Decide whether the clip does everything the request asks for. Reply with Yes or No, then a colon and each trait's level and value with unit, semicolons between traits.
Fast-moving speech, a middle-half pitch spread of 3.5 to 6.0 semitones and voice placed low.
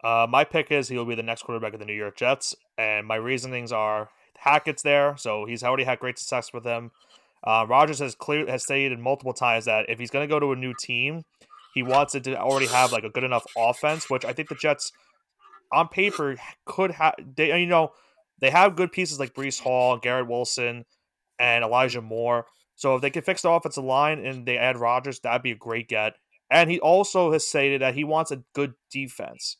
Yes: fast, 220 wpm; average, 3.9 semitones; low, 130 Hz